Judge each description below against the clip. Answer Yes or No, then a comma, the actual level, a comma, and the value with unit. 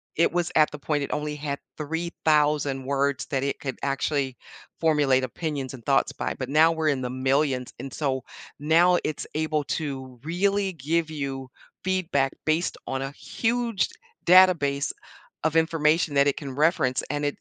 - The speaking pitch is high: No, medium, 150 Hz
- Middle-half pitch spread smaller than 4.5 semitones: Yes, average, 3.0 semitones